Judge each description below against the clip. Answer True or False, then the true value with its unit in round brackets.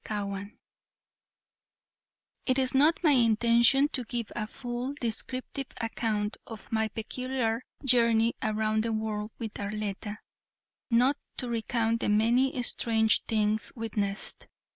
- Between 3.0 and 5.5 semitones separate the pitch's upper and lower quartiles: False (2.4 semitones)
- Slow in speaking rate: True (120 wpm)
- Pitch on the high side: True (225 Hz)